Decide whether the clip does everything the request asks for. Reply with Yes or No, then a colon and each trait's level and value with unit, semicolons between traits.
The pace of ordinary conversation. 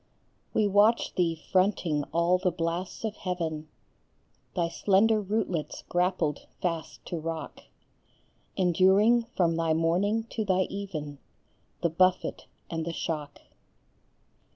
No: slow, 115 wpm